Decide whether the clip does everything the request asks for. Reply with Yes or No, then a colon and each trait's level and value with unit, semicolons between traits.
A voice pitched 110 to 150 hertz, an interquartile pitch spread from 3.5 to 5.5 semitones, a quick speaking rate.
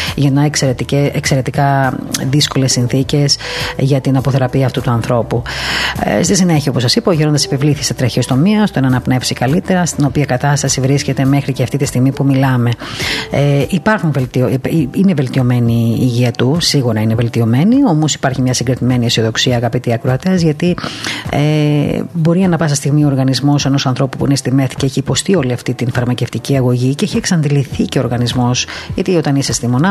No: low, 135 Hz; average, 2.7 semitones; fast, 175 wpm